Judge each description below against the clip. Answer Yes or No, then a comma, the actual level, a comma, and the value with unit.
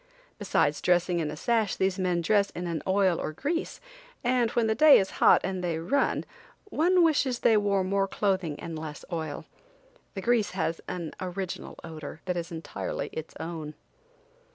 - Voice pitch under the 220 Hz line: Yes, medium, 185 Hz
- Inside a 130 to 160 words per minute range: No, average, 175 wpm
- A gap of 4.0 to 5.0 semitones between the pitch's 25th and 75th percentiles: Yes, average, 4.6 semitones